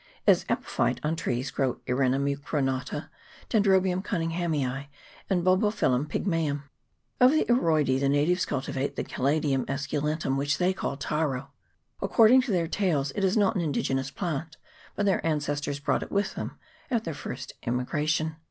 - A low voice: No, medium, 150 Hz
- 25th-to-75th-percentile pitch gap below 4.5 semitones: No, average, 4.9 semitones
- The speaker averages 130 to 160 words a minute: Yes, average, 150 wpm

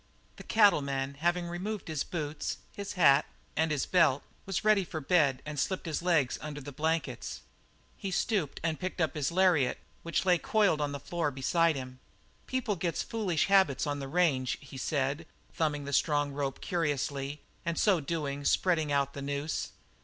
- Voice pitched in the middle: Yes, medium, 155 Hz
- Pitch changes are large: No, average, 3.9 semitones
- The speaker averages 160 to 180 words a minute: Yes, average, 175 wpm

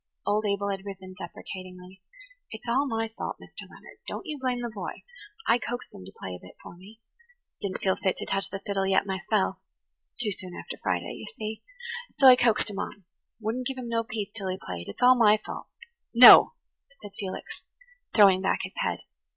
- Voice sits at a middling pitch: No, high, 205 Hz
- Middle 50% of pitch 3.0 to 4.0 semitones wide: Yes, average, 3.4 semitones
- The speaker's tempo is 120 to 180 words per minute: No, average, 195 wpm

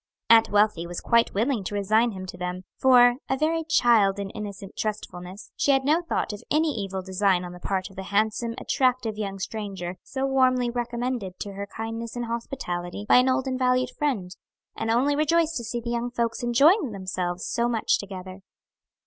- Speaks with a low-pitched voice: No, high, 225 Hz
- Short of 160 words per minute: No, average, 190 wpm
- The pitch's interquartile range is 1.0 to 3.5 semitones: No, average, 4.5 semitones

